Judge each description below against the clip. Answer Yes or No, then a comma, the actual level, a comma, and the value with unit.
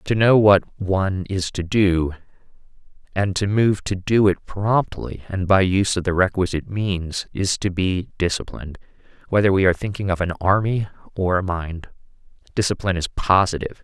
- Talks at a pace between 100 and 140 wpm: No, average, 165 wpm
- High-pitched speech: No, very low, 95 Hz